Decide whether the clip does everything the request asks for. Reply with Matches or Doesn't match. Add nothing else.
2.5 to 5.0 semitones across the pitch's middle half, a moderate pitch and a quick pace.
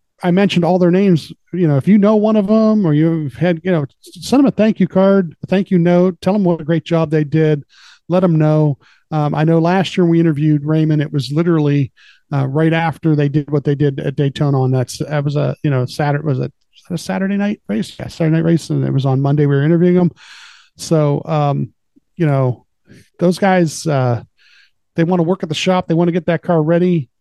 Matches